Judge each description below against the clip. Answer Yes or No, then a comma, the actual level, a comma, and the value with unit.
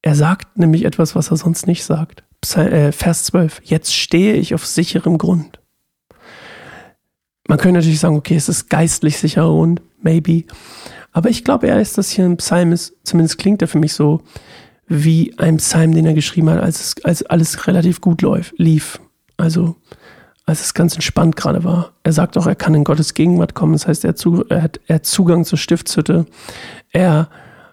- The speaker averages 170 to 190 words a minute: Yes, average, 175 wpm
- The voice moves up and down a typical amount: No, narrow, 1.6 semitones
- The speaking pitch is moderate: Yes, medium, 165 Hz